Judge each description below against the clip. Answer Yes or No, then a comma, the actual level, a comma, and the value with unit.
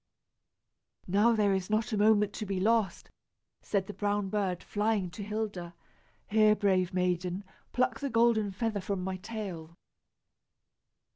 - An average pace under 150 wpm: Yes, average, 140 wpm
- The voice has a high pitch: Yes, high, 205 Hz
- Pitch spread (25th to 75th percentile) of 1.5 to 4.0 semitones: Yes, narrow, 2.5 semitones